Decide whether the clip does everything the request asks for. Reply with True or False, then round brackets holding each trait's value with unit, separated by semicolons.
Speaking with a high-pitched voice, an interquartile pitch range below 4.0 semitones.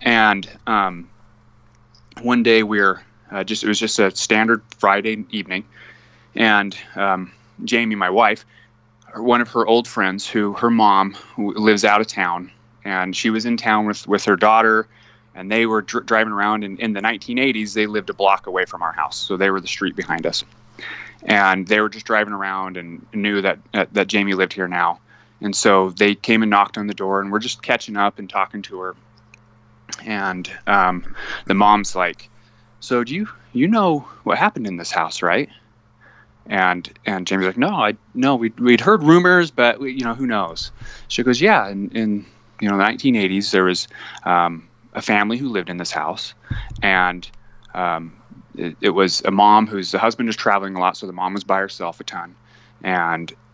False (105 Hz; 2.8 semitones)